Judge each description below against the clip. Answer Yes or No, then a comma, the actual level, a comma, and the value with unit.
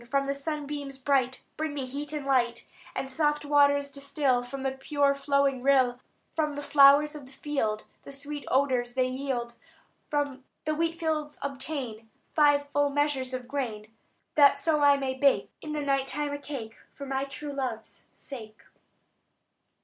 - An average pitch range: No, narrow, 1.9 semitones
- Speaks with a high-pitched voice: Yes, very high, 280 Hz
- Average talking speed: Yes, average, 165 wpm